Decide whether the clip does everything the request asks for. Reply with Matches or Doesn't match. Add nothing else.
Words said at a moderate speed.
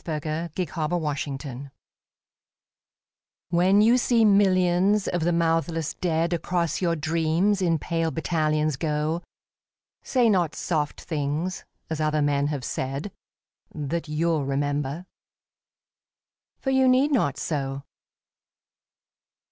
Doesn't match